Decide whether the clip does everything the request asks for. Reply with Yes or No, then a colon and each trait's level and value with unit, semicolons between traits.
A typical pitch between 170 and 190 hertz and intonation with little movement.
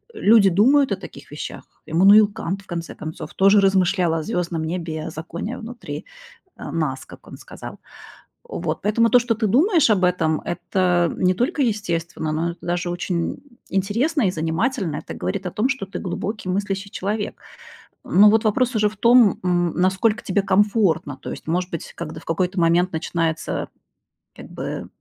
No: medium, 185 Hz; average, 4.1 semitones